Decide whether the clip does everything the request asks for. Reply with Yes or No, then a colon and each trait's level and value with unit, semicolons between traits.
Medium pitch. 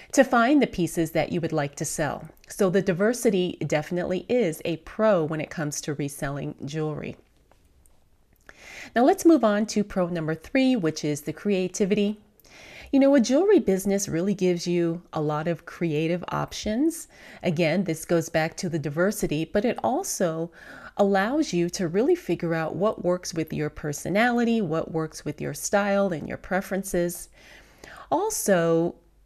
Yes: medium, 180 Hz